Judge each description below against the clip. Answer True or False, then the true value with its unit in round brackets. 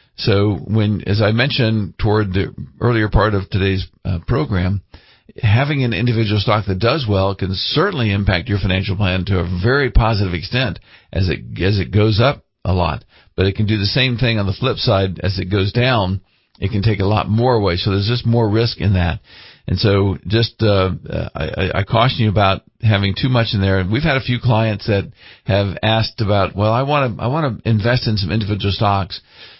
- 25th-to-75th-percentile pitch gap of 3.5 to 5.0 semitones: False (3.1 semitones)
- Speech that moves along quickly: True (210 wpm)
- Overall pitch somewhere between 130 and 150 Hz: False (105 Hz)